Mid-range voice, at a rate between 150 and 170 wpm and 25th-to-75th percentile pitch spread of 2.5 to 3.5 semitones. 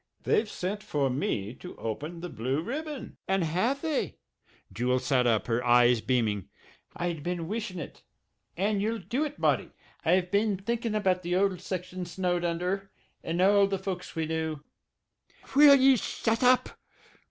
No: medium, 180 Hz; average, 165 wpm; wide, 5.4 semitones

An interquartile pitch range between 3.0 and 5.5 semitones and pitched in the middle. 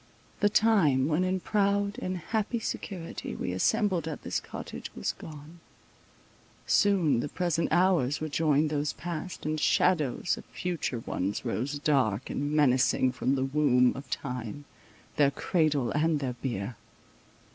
Yes: average, 5.2 semitones; medium, 150 Hz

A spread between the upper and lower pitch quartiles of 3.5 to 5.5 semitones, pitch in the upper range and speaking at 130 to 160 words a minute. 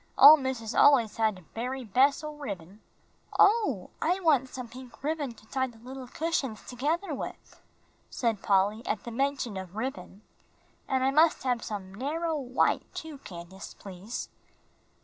Yes: average, 4.9 semitones; very high, 255 Hz; average, 155 wpm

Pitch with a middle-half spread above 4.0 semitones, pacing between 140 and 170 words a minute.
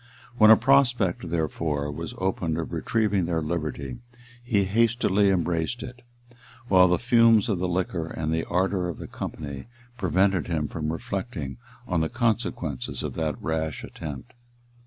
Yes: average, 4.9 semitones; average, 150 wpm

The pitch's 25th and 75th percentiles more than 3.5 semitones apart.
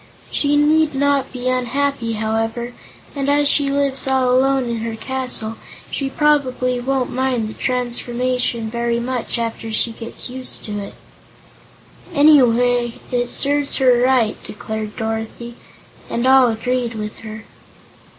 No: average, 2.7 semitones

